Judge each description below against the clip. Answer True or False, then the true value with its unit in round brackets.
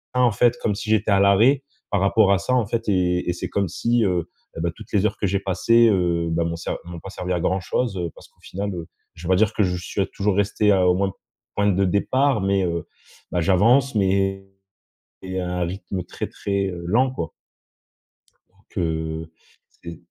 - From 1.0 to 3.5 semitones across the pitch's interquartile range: True (2.7 semitones)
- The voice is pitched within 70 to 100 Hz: True (95 Hz)